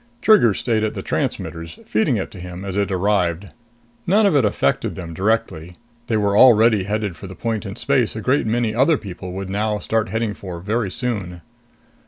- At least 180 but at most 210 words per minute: Yes, average, 195 wpm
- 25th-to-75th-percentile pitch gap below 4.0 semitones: Yes, average, 3.5 semitones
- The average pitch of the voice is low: Yes, low, 105 Hz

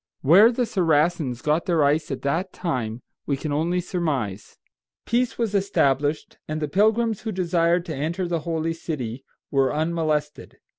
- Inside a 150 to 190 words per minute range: Yes, average, 155 wpm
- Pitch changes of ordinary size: Yes, average, 3.8 semitones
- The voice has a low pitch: No, medium, 160 Hz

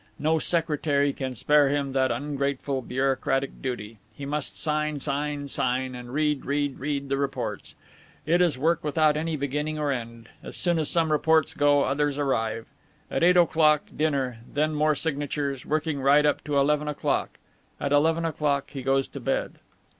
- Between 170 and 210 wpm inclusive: Yes, average, 175 wpm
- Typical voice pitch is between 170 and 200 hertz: No, medium, 145 Hz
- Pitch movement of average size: No, narrow, 1.9 semitones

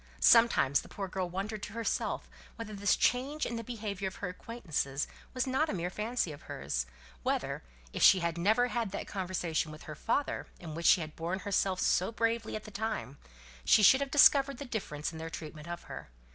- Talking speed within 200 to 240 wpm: Yes, fast, 205 wpm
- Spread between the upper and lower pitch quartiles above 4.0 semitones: Yes, average, 5.3 semitones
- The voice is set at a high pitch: Yes, high, 200 Hz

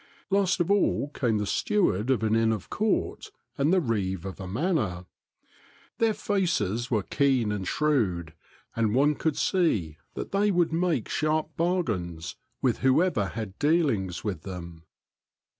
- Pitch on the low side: Yes, low, 120 Hz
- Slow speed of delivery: No, average, 150 wpm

